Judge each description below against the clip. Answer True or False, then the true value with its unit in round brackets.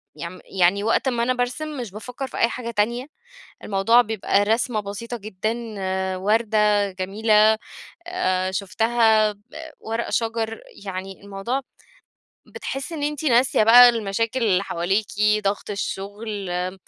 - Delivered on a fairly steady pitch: False (3.1 semitones)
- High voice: True (215 Hz)